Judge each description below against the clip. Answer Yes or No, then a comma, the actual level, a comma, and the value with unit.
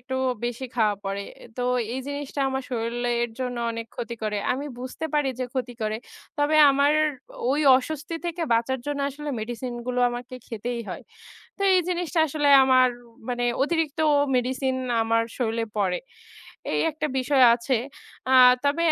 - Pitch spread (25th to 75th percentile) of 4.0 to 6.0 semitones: No, average, 3.3 semitones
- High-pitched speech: Yes, very high, 255 Hz